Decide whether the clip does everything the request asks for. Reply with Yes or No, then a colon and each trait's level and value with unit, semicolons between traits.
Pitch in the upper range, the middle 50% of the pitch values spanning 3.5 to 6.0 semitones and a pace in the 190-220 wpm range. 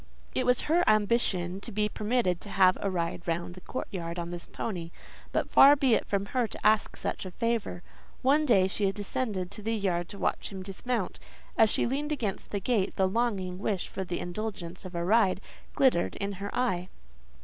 Yes: high, 200 Hz; average, 4.1 semitones; average, 200 wpm